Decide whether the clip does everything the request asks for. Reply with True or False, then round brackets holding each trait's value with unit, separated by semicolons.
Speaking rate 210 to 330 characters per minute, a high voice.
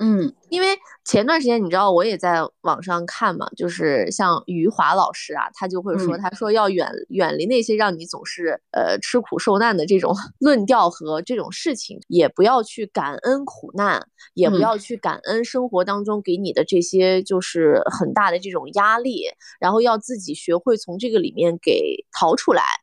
True (275 characters per minute; 210 Hz)